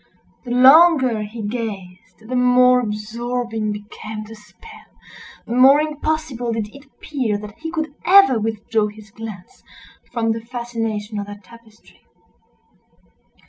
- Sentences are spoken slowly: Yes, slow, 125 wpm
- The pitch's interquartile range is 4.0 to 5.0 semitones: No, average, 3.1 semitones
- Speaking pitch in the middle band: No, high, 230 Hz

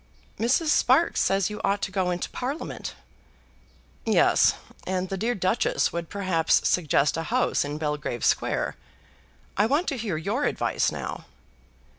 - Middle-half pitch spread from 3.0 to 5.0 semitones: No, wide, 5.6 semitones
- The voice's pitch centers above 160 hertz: Yes, high, 190 Hz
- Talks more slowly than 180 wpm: Yes, average, 145 wpm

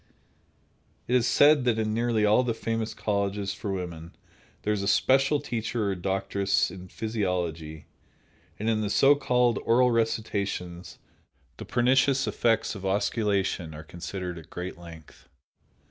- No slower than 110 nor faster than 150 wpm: Yes, average, 145 wpm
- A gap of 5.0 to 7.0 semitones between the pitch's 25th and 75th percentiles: No, average, 4.2 semitones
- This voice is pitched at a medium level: No, low, 105 Hz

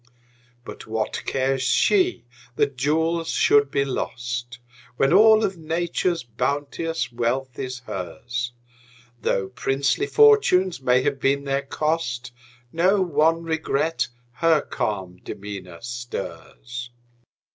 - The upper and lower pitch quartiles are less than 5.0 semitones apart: No, average, 5.3 semitones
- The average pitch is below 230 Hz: Yes, low, 135 Hz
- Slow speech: Yes, slow, 110 wpm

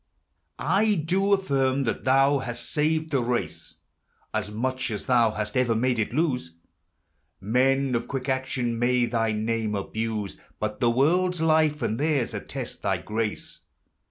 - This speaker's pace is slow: No, average, 150 wpm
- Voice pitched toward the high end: No, low, 125 Hz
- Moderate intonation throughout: Yes, average, 4.3 semitones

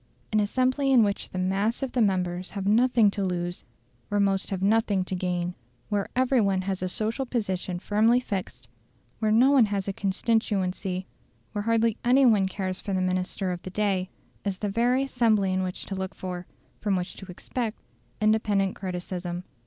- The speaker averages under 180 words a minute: No, average, 185 wpm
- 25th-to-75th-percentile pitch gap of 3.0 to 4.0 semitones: Yes, average, 3.3 semitones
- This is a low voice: No, high, 200 Hz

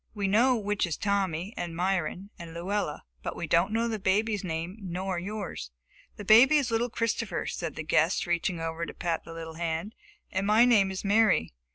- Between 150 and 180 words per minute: No, average, 195 wpm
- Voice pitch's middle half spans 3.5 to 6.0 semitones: Yes, average, 4.0 semitones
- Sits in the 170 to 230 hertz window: Yes, high, 190 Hz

